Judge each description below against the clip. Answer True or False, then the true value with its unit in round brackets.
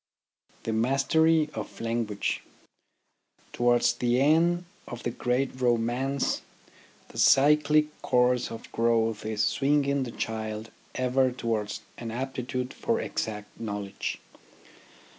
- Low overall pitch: True (125 Hz)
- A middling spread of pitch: True (3.2 semitones)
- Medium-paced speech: False (105 wpm)